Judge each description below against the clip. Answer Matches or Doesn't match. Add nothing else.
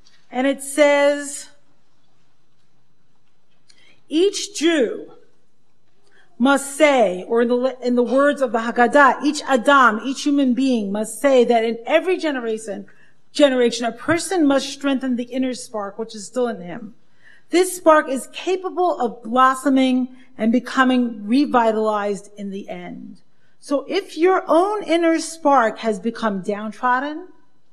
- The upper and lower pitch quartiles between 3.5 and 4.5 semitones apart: Matches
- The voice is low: Doesn't match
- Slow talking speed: Matches